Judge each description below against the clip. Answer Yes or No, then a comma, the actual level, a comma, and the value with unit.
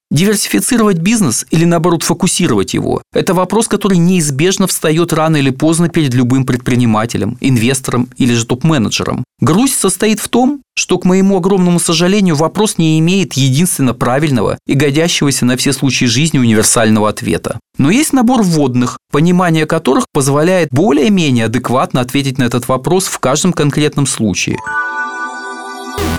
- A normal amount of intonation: No, wide, 6.2 semitones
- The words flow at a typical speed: Yes, average, 135 wpm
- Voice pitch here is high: No, medium, 160 Hz